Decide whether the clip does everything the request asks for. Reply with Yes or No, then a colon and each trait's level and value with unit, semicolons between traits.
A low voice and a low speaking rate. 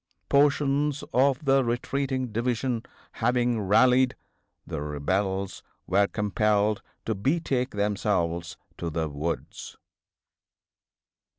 Yes: low, 115 Hz; slow, 90 wpm